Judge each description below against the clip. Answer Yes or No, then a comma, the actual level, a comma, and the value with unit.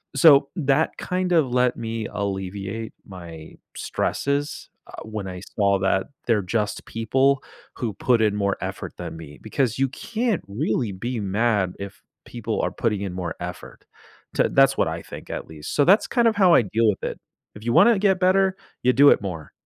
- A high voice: No, low, 115 Hz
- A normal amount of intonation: No, wide, 6.2 semitones